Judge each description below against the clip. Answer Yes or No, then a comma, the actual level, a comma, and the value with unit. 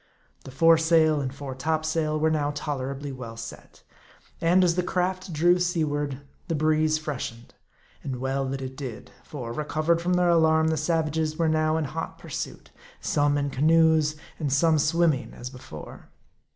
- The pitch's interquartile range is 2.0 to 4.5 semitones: Yes, average, 2.9 semitones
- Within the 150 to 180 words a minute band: Yes, average, 165 wpm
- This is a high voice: No, medium, 155 Hz